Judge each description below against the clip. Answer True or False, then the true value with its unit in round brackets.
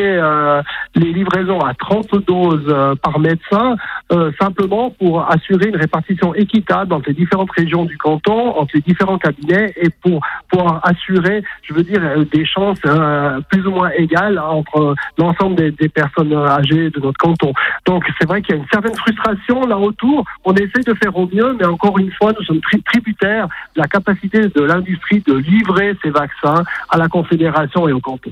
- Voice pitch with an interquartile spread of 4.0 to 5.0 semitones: True (4.3 semitones)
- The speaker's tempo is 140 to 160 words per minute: False (175 wpm)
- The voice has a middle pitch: True (180 Hz)